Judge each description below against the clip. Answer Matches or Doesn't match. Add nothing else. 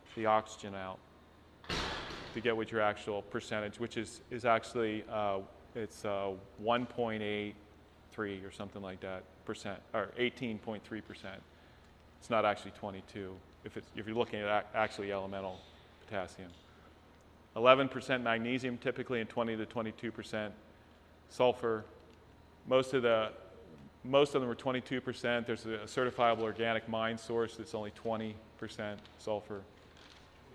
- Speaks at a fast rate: Doesn't match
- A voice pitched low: Matches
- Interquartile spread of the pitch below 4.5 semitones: Matches